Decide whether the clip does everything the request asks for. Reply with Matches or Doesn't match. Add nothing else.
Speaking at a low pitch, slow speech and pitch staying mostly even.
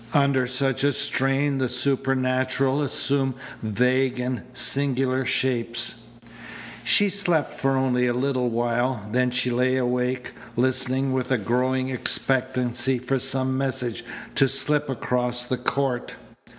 Matches